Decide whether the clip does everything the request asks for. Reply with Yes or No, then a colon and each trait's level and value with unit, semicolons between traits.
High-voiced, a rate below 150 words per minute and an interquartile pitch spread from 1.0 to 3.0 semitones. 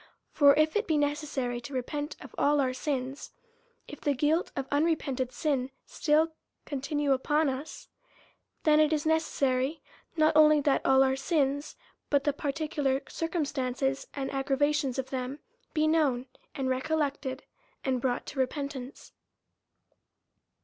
Yes: very high, 285 Hz; average, 140 wpm; narrow, 2.4 semitones